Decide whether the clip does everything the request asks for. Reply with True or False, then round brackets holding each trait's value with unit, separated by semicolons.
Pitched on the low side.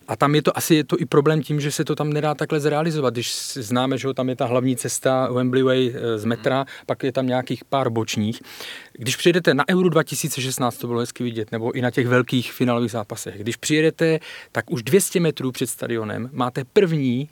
True (130 Hz)